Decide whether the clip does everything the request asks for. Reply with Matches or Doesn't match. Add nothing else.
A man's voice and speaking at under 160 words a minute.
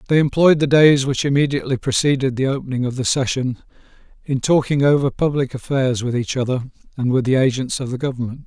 Doesn't match